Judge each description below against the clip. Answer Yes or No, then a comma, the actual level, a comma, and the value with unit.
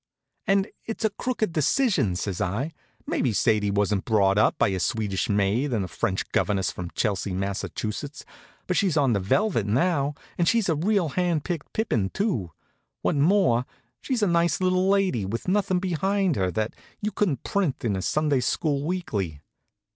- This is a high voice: No, medium, 140 Hz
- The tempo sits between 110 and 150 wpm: No, average, 170 wpm